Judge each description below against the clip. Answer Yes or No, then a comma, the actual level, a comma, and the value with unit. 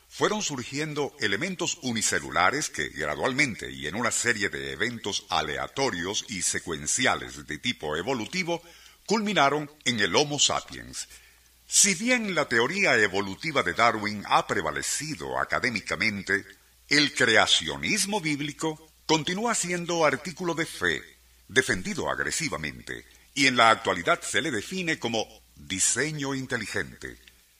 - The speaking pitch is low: Yes, low, 120 Hz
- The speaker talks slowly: Yes, slow, 115 wpm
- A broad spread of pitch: Yes, wide, 8.8 semitones